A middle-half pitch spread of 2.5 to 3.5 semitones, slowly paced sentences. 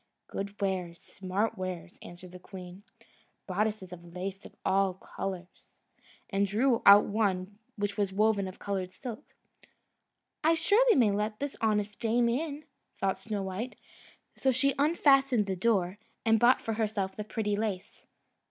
No: average, 3.2 semitones; average, 145 wpm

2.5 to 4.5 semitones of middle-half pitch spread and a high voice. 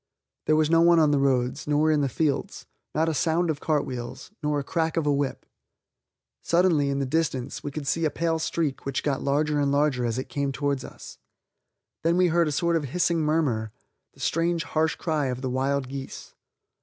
No: average, 2.8 semitones; medium, 150 Hz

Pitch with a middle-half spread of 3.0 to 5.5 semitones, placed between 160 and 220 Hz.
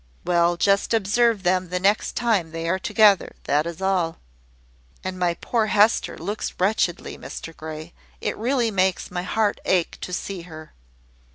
Yes: average, 3.5 semitones; medium, 185 Hz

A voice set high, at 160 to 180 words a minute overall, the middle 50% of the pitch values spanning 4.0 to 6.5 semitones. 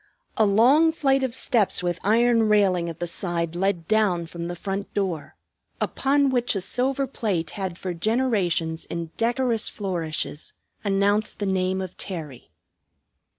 No: high, 195 Hz; average, 150 wpm; average, 5.0 semitones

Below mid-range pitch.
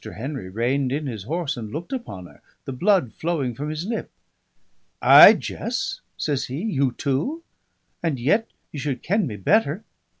No: medium, 145 Hz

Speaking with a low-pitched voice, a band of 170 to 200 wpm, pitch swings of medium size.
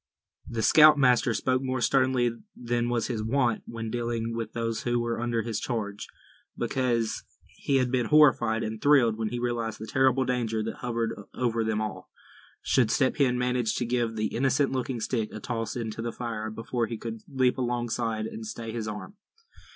No: low, 120 Hz; average, 180 wpm; narrow, 2.0 semitones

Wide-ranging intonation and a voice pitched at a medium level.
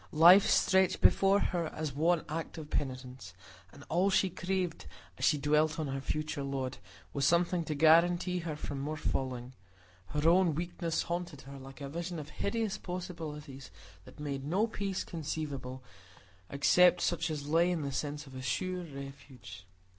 No: average, 4.1 semitones; medium, 155 Hz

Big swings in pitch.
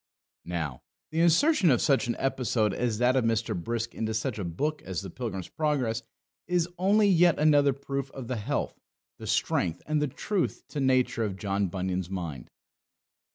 Yes: wide, 6.7 semitones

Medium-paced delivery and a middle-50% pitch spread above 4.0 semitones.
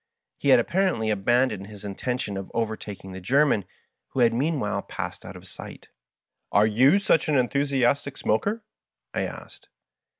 Yes: average, 155 wpm; average, 5.2 semitones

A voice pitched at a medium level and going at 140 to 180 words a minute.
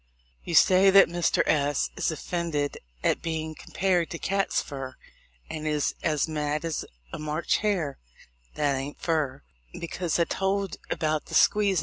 Yes: medium, 160 Hz; average, 150 wpm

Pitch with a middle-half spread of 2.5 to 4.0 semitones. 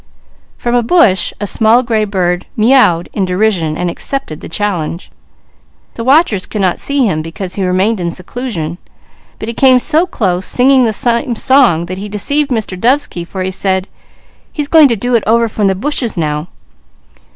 No: wide, 5.4 semitones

